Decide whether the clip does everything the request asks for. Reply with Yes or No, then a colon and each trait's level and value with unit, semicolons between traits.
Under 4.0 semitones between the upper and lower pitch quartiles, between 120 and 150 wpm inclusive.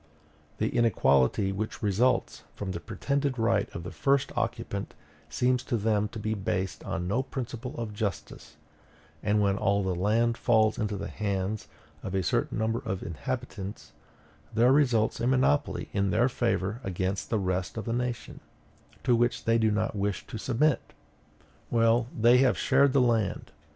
No: average, 3.5 semitones; average, 165 wpm